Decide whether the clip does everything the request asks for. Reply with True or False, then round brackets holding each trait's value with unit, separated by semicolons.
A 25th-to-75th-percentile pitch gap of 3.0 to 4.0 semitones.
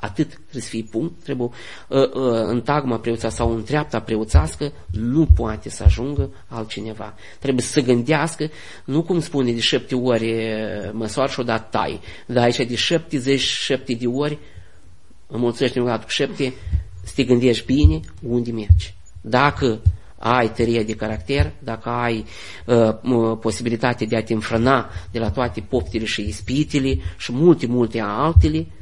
True (3.5 semitones)